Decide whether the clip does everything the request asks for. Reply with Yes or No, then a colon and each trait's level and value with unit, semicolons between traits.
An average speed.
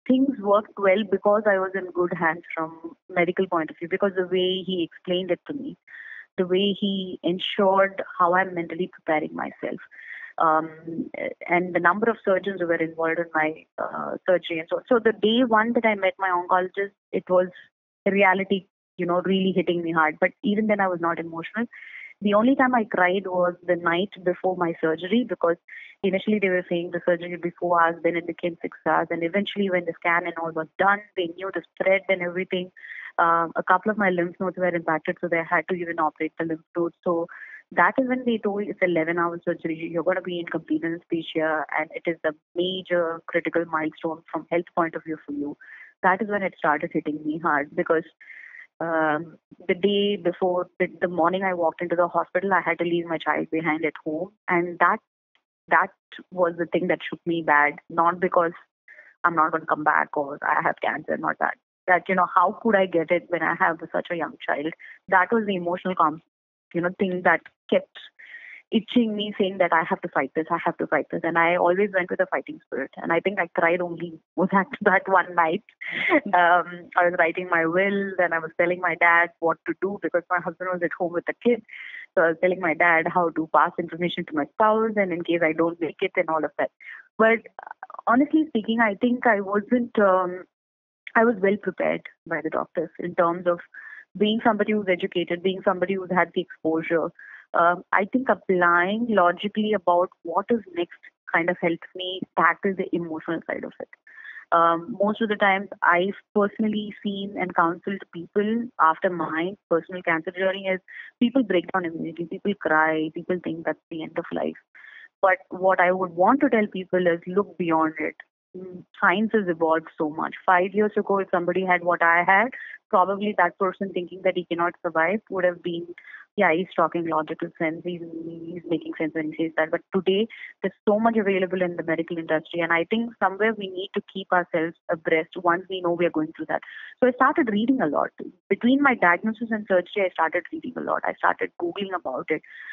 No: fast, 210 wpm